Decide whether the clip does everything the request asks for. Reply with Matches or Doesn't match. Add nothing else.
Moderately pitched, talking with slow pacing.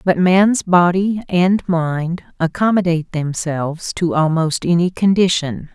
Matches